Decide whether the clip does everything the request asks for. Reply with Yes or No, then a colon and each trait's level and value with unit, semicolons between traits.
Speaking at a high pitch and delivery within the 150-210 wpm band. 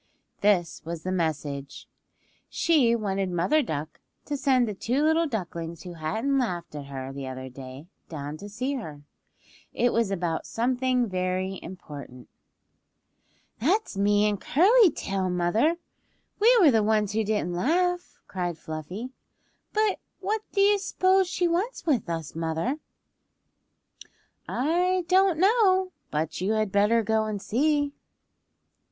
No: high, 215 Hz; average, 140 wpm